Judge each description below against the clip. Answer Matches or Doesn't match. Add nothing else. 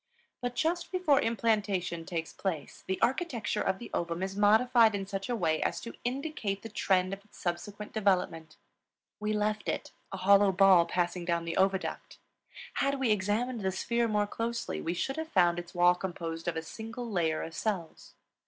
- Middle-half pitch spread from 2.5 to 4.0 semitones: Doesn't match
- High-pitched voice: Matches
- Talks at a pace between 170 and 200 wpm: Matches